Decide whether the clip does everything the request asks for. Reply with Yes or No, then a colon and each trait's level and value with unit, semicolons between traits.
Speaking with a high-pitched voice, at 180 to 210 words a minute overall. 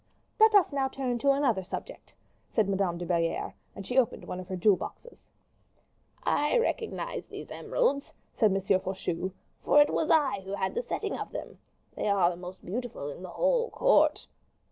Yes: high, 215 Hz; average, 185 wpm